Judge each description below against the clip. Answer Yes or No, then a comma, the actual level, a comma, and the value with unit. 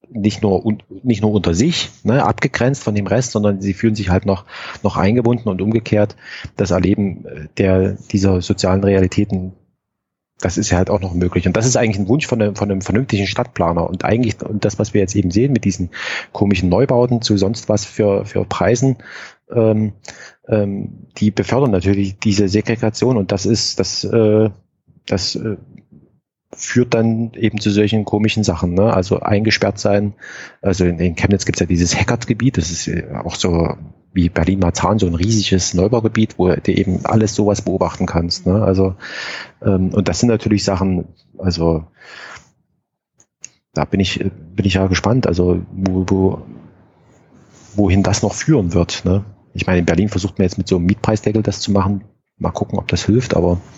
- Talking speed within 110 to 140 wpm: No, average, 180 wpm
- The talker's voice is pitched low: Yes, low, 100 Hz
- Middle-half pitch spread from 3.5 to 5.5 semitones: No, average, 2.8 semitones